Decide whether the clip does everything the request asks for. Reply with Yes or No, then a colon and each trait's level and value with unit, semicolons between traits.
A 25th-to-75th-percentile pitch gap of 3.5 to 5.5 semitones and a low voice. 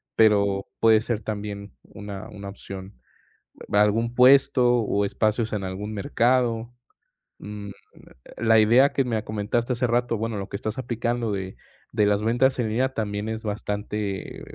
No: narrow, 2.5 semitones; low, 110 Hz